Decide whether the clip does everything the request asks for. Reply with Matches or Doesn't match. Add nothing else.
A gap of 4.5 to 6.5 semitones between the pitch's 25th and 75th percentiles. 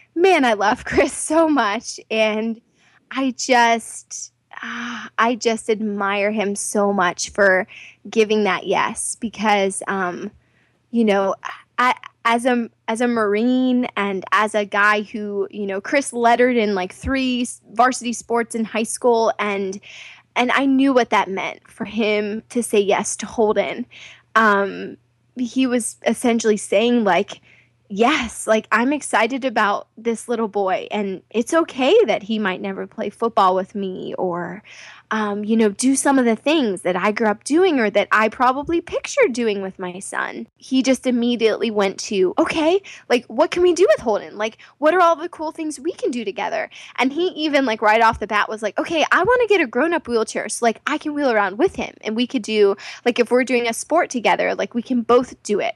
Doesn't match